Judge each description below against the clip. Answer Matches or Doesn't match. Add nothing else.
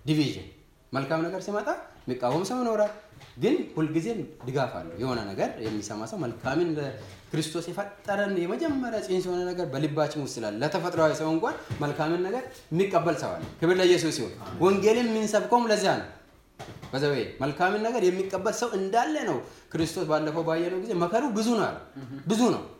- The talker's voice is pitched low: Doesn't match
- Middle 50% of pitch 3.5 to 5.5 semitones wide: Matches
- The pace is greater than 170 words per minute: Doesn't match